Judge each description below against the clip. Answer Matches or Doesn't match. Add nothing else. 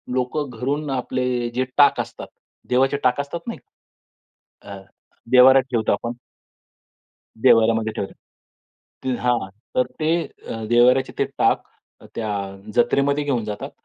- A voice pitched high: Doesn't match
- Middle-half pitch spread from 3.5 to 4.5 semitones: Doesn't match